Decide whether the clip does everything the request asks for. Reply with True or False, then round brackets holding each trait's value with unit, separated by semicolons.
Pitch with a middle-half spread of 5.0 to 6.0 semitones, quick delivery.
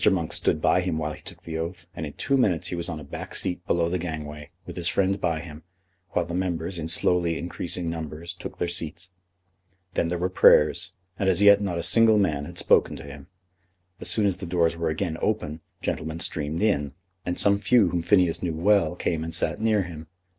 False (2.6 semitones; 220 wpm)